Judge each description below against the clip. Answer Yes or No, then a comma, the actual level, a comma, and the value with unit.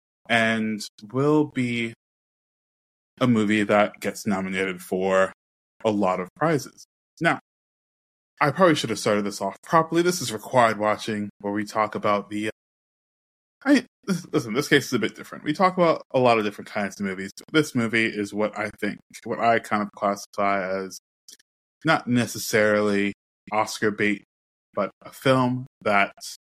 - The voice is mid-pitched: No, low, 105 Hz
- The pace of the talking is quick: No, average, 160 wpm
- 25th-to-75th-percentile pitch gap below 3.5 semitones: Yes, average, 3.0 semitones